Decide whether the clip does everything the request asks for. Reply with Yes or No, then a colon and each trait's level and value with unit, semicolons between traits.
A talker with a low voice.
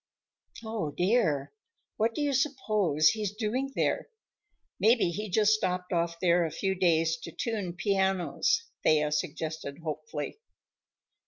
No: medium, 180 Hz